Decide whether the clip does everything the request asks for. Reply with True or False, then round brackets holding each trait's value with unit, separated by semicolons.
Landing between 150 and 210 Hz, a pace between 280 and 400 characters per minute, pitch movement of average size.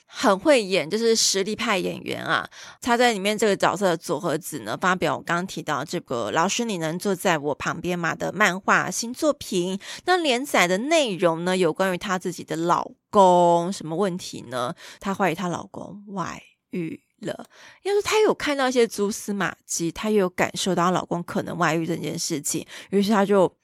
True (190 Hz; 285 characters per minute; 3.9 semitones)